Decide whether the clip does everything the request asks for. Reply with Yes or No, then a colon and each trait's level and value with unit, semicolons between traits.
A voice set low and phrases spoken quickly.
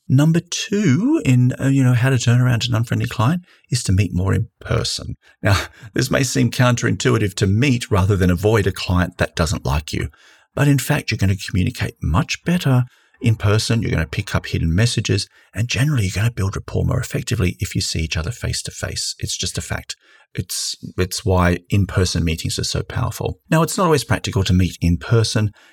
Yes: low, 115 Hz; fast, 210 wpm